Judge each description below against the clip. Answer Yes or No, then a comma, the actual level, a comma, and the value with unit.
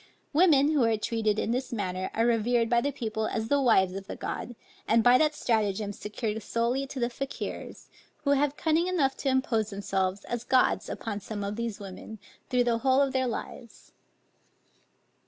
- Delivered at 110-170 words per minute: No, average, 185 wpm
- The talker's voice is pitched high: Yes, high, 235 Hz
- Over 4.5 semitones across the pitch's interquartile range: No, average, 3.8 semitones